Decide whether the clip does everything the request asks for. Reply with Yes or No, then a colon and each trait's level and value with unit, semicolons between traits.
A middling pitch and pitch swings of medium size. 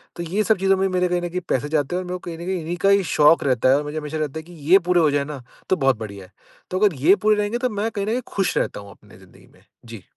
Yes: medium, 175 Hz; average, 4.8 semitones